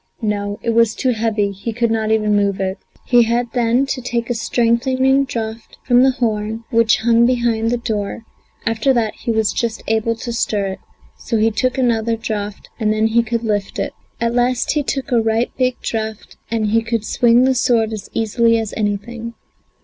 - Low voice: No, high, 230 Hz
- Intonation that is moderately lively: No, narrow, 1.7 semitones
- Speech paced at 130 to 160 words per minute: No, average, 195 wpm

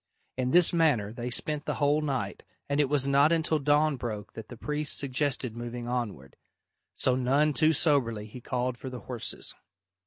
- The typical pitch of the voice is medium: No, low, 130 Hz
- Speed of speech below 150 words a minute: No, average, 180 wpm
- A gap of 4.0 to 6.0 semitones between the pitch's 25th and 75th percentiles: No, average, 3.6 semitones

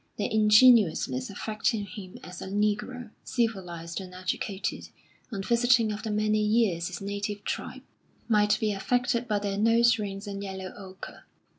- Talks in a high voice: Yes, high, 210 Hz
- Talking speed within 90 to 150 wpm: Yes, average, 145 wpm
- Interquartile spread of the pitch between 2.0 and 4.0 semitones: Yes, narrow, 2.4 semitones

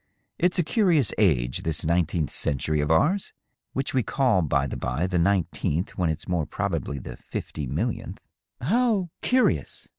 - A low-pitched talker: Yes, very low, 90 Hz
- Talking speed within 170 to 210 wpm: Yes, average, 175 wpm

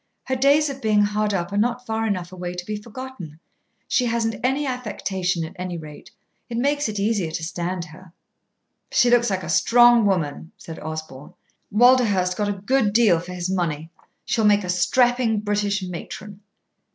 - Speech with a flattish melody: No, average, 4.9 semitones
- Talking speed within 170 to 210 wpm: Yes, average, 175 wpm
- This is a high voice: Yes, high, 205 Hz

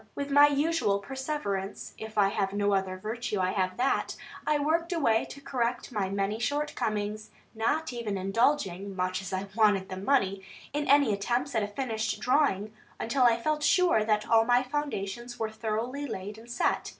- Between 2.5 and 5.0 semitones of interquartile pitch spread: No, wide, 5.5 semitones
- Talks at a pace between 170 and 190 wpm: Yes, average, 175 wpm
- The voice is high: Yes, high, 225 Hz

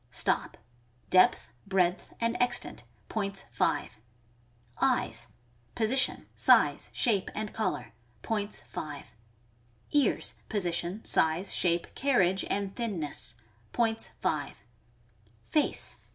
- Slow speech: Yes, slow, 100 wpm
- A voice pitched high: Yes, high, 195 Hz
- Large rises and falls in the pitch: No, average, 4.6 semitones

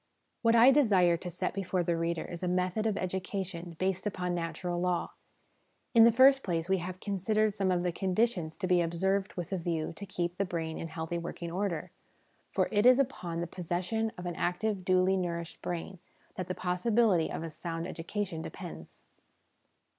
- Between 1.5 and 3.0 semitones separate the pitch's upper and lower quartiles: Yes, narrow, 2.6 semitones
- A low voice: No, medium, 180 Hz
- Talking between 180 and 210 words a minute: Yes, average, 185 wpm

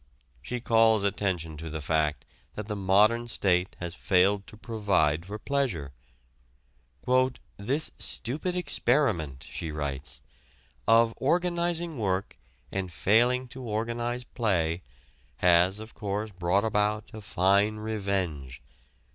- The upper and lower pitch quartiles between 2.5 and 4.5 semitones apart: No, average, 4.9 semitones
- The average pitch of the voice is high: No, low, 105 Hz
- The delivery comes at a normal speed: No, slow, 115 wpm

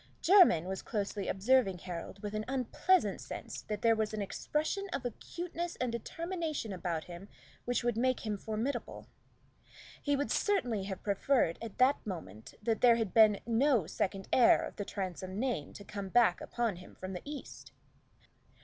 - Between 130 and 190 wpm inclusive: Yes, average, 165 wpm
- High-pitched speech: Yes, high, 220 Hz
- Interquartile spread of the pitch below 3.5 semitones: No, average, 5.1 semitones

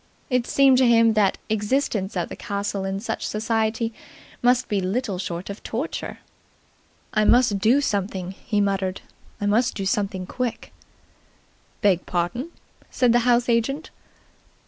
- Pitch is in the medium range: No, high, 215 Hz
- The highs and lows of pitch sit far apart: No, average, 3.7 semitones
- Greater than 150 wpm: No, average, 145 wpm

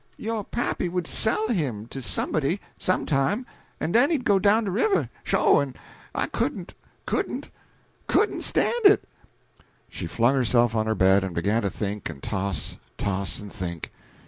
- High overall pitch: No, low, 130 Hz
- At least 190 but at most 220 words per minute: No, average, 165 wpm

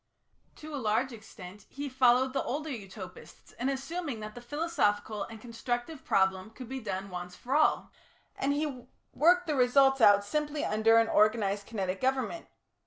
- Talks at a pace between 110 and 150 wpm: No, average, 165 wpm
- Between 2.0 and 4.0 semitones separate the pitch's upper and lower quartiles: No, average, 4.9 semitones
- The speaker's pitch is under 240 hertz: No, high, 245 Hz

